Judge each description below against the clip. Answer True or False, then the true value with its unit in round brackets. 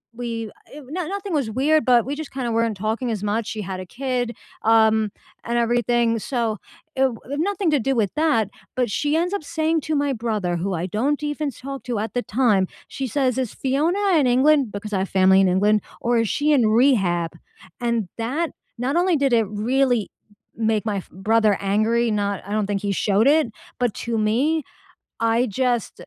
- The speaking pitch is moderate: False (235 Hz)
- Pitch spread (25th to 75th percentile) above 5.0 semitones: False (4.5 semitones)